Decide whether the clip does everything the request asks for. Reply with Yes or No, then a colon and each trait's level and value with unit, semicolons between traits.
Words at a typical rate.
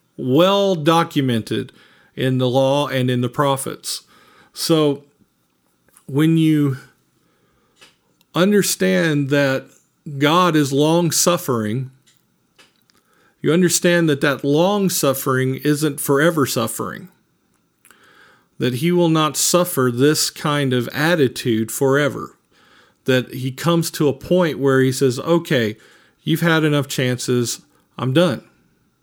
No: slow, 110 wpm